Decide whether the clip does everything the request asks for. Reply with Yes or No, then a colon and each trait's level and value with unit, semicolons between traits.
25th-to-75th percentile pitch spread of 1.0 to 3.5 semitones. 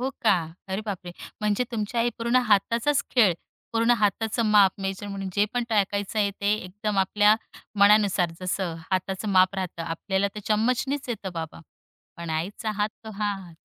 Yes: narrow, 2.5 semitones